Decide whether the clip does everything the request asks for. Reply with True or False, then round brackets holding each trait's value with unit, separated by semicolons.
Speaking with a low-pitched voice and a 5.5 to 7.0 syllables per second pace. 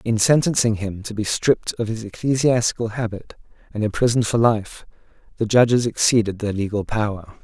True (110 Hz; 5.6 syllables/s)